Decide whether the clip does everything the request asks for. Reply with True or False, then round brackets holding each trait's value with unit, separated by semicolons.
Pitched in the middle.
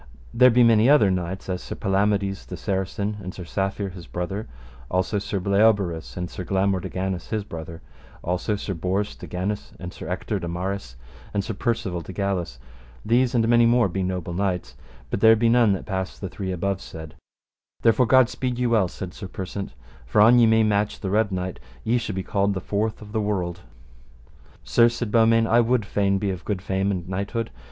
False (100 Hz)